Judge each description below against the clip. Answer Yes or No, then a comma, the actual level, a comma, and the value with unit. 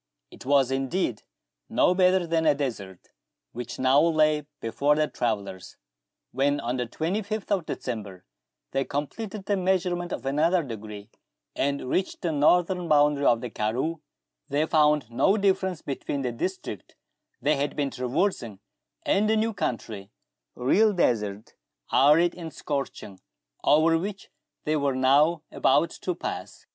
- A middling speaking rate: Yes, average, 145 wpm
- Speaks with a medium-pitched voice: Yes, medium, 145 Hz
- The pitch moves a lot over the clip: Yes, wide, 5.8 semitones